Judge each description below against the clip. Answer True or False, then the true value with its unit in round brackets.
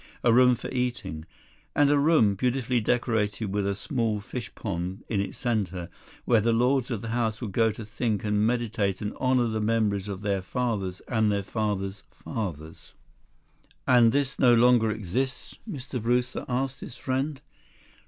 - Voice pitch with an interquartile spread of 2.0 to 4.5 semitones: True (3.4 semitones)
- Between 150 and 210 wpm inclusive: True (165 wpm)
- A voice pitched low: True (115 Hz)